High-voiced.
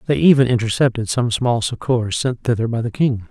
No: low, 115 Hz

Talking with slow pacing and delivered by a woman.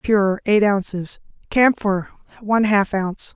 Yes: slow, 125 wpm; female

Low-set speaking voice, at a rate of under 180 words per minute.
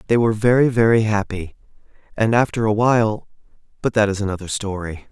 Yes: low, 110 Hz; average, 155 wpm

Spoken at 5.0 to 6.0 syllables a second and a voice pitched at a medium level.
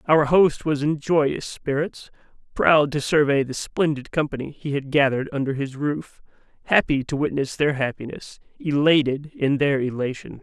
No: 4.8 syllables/s; medium, 145 Hz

